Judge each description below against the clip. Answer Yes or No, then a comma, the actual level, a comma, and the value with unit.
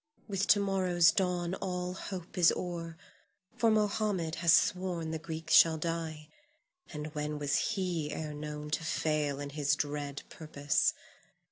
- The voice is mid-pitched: Yes, medium, 165 Hz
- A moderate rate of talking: Yes, average, 145 wpm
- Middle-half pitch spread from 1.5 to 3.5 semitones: Yes, average, 3.1 semitones